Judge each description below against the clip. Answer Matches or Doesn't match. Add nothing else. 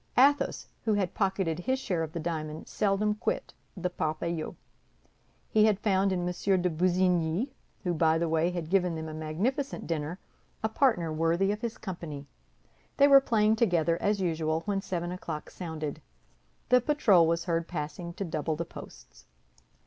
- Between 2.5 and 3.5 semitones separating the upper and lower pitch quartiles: Doesn't match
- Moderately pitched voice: Matches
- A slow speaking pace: Doesn't match